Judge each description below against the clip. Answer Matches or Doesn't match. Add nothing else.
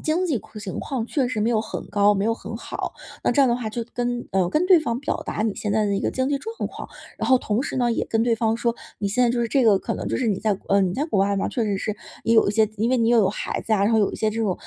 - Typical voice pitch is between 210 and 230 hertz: Matches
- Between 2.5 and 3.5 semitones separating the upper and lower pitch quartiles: Matches